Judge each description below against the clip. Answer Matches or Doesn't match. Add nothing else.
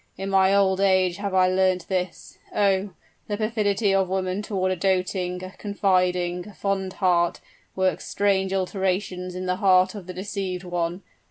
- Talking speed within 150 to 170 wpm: Matches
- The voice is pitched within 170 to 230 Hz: Matches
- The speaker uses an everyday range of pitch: Doesn't match